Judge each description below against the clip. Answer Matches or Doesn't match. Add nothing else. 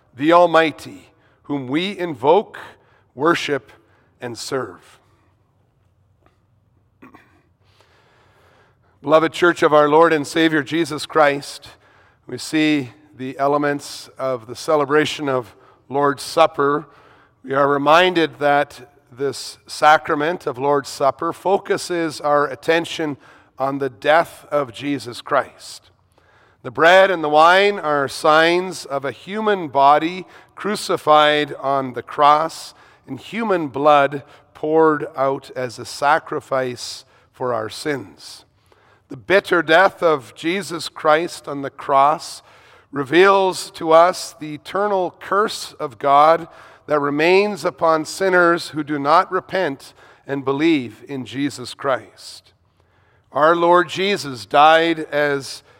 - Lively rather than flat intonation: Doesn't match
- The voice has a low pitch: Doesn't match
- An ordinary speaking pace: Doesn't match